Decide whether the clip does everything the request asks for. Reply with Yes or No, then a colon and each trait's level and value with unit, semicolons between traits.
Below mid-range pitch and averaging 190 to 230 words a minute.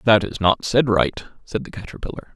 Yes: low, 105 Hz; fast, 205 wpm